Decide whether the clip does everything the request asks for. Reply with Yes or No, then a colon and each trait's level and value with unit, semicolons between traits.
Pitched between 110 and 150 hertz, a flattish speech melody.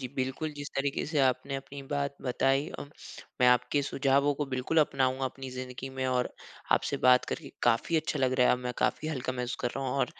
Yes: low, 135 Hz; narrow, 1.8 semitones